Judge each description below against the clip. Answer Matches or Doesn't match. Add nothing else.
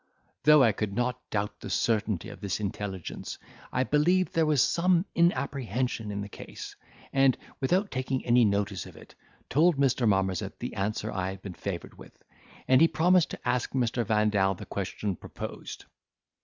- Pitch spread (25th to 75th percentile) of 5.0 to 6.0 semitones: Matches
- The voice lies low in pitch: Matches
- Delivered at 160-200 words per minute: Matches